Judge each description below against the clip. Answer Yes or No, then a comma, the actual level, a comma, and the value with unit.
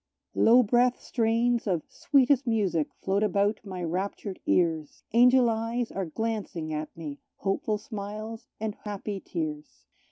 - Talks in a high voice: Yes, high, 210 Hz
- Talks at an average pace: No, slow, 130 wpm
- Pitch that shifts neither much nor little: Yes, average, 4.2 semitones